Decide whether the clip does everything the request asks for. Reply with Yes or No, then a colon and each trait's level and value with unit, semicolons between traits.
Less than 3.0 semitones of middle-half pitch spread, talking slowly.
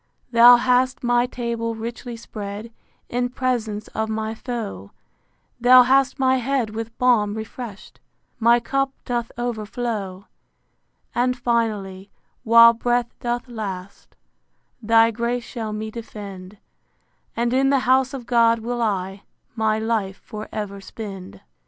Yes: narrow, 2.4 semitones; slow, 125 wpm